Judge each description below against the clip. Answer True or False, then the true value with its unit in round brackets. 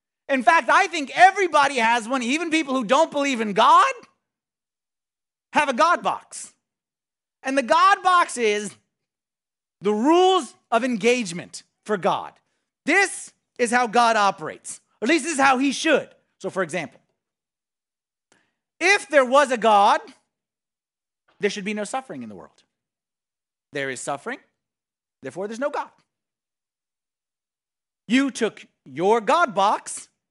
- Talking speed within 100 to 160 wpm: True (140 wpm)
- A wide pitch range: True (6.7 semitones)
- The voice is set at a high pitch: True (260 Hz)